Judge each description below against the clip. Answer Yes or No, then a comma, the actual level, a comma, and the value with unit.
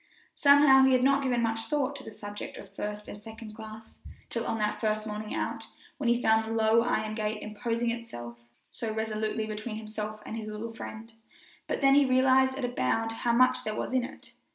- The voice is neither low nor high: No, high, 225 Hz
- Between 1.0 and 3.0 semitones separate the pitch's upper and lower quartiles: Yes, narrow, 2.6 semitones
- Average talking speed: No, fast, 210 wpm